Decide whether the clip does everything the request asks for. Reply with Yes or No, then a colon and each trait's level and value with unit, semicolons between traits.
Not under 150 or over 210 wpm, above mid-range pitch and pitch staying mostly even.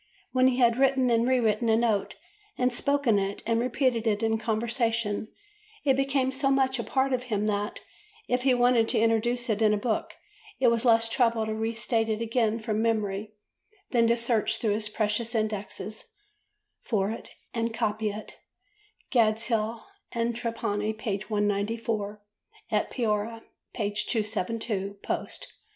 Yes: average, 160 wpm; high, 225 Hz; narrow, 2.0 semitones